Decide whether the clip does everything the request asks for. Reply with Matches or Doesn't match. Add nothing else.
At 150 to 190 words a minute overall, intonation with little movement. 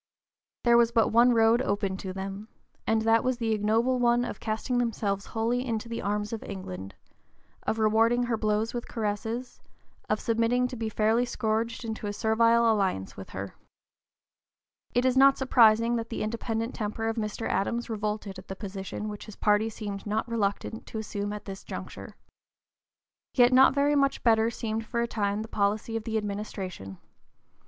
Matches